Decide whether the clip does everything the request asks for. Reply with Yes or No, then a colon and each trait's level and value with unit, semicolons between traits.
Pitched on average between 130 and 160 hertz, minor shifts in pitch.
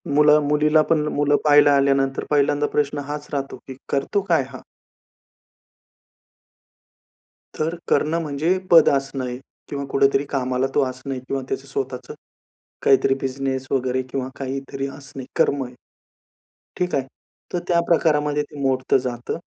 Yes: medium, 140 Hz; narrow, 1.9 semitones